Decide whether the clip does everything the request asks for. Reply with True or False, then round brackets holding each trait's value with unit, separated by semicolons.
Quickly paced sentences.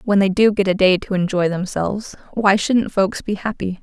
True (220 wpm)